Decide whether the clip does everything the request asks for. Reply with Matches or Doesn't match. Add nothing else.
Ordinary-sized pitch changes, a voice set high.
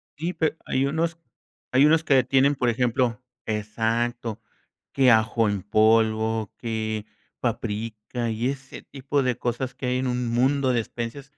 Doesn't match